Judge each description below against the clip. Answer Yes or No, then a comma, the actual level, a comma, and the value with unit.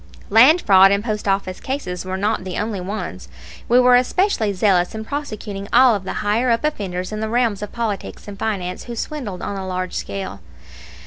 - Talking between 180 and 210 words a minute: Yes, average, 195 wpm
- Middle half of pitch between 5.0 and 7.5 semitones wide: No, average, 3.7 semitones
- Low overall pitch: No, high, 210 Hz